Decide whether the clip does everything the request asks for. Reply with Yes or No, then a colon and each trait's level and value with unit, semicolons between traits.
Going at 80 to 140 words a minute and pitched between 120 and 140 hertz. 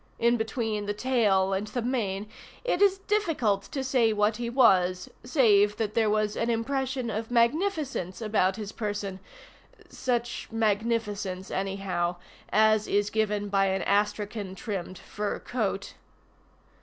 No: slow, 135 wpm; high, 215 Hz